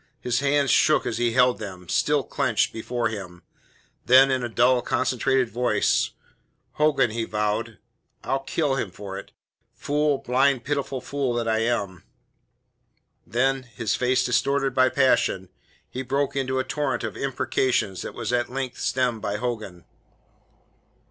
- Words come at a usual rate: Yes, average, 150 wpm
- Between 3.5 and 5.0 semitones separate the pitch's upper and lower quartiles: No, average, 3.0 semitones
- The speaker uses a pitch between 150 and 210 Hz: No, low, 125 Hz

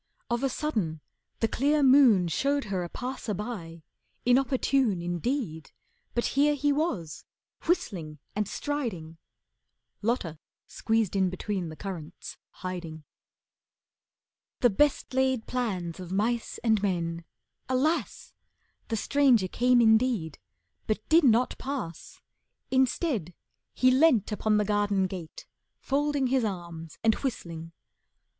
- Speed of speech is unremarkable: No, slow, 120 wpm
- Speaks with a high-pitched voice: Yes, high, 220 Hz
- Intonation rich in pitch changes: Yes, wide, 6.8 semitones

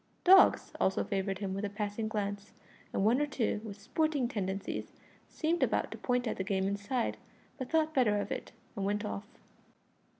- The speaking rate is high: No, average, 185 wpm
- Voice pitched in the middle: No, high, 210 Hz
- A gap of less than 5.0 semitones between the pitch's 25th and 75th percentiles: Yes, average, 4.0 semitones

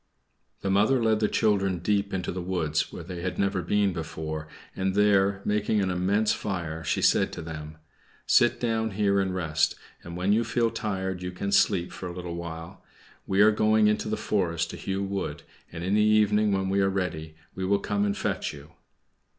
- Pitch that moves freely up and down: No, average, 3.0 semitones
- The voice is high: No, very low, 95 Hz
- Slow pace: No, average, 200 wpm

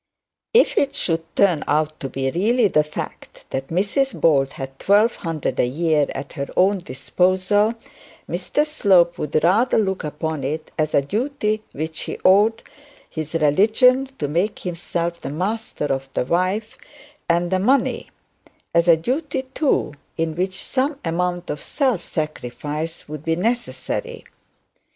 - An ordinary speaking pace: Yes, average, 150 wpm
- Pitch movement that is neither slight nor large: No, wide, 5.8 semitones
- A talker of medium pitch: Yes, medium, 175 Hz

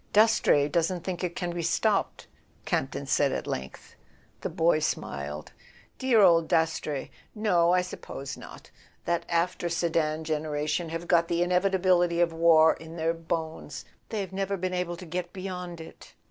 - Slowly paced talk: No, average, 160 wpm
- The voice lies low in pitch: No, medium, 170 Hz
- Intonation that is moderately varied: No, narrow, 2.0 semitones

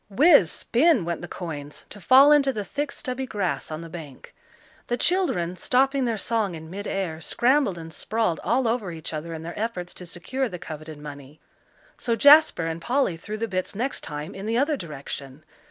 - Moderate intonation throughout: No, wide, 7.6 semitones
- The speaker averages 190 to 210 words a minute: Yes, average, 195 wpm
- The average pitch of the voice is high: Yes, high, 195 Hz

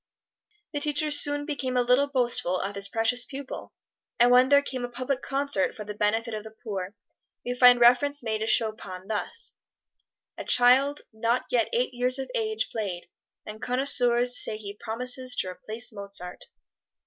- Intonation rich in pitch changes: No, average, 3.1 semitones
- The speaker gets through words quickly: No, average, 170 wpm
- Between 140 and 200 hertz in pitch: No, high, 245 Hz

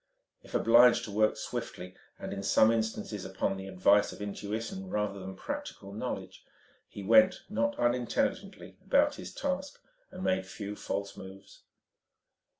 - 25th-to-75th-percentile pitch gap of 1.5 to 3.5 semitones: Yes, average, 3.1 semitones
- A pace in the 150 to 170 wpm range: No, average, 140 wpm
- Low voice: Yes, low, 105 Hz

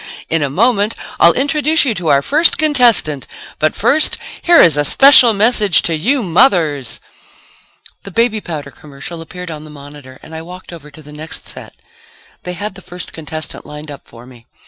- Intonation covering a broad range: Yes, wide, 7.3 semitones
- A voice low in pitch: No, medium, 170 Hz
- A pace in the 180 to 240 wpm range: Yes, average, 190 wpm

